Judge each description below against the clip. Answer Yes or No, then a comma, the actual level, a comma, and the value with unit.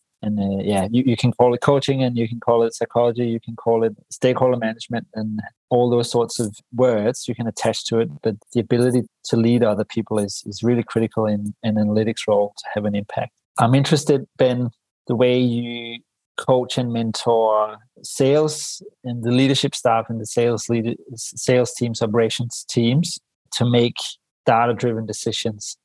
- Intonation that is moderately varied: No, narrow, 1.8 semitones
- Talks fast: No, average, 180 wpm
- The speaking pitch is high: No, low, 120 Hz